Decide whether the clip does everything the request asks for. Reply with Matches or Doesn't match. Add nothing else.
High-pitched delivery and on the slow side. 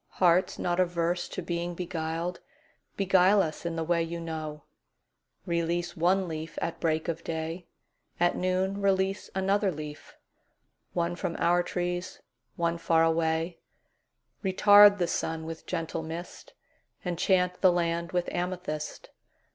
Doesn't match